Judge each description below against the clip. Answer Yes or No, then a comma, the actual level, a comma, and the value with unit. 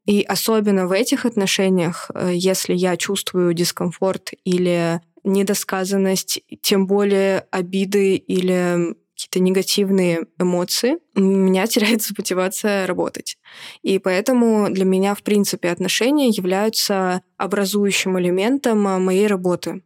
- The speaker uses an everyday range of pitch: No, narrow, 1.8 semitones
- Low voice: No, high, 190 Hz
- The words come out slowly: Yes, slow, 105 wpm